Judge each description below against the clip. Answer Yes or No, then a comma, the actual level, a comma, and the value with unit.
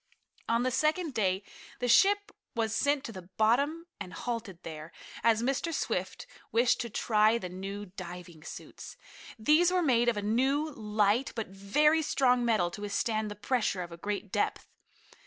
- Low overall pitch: No, high, 225 Hz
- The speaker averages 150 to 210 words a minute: Yes, average, 170 wpm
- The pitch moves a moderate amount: Yes, average, 4.8 semitones